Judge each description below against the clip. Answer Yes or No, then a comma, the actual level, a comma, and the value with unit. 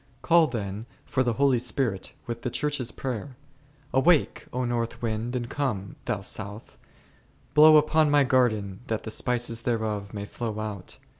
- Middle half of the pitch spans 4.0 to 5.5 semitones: No, average, 3.5 semitones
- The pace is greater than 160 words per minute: No, average, 155 wpm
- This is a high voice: No, low, 120 Hz